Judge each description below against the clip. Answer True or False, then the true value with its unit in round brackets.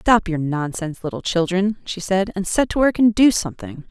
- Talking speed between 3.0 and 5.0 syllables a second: False (5.4 syllables/s)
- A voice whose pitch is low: False (190 Hz)